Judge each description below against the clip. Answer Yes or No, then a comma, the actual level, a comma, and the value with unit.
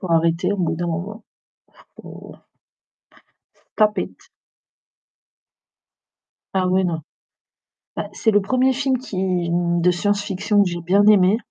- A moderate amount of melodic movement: Yes, average, 3.2 semitones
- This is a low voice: No, high, 190 Hz